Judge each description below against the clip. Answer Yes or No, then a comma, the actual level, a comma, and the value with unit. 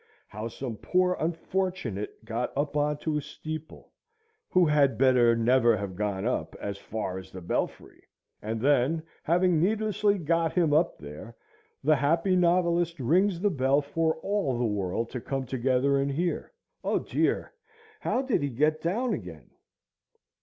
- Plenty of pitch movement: Yes, wide, 6.5 semitones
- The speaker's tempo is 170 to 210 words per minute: No, average, 155 wpm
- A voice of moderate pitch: Yes, medium, 145 Hz